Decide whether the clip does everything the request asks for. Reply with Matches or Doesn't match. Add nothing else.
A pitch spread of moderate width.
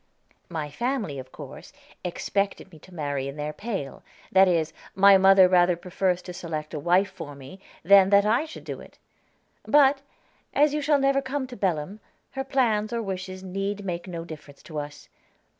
Matches